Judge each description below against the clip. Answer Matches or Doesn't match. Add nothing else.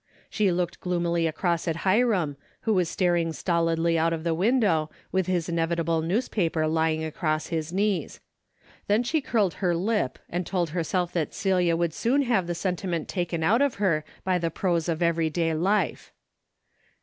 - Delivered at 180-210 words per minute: Doesn't match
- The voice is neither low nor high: Matches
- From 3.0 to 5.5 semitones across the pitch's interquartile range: Doesn't match